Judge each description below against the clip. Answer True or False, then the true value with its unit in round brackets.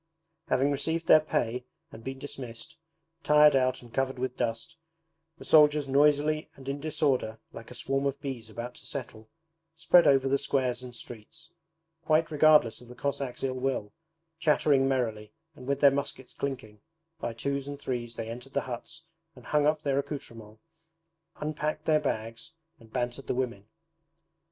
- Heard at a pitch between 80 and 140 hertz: True (135 Hz)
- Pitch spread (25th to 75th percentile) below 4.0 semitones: True (3.6 semitones)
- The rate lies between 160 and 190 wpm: True (165 wpm)